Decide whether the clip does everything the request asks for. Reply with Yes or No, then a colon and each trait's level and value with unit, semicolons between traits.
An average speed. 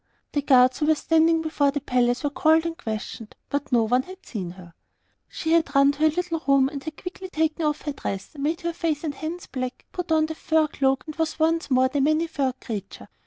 No: fast, 230 wpm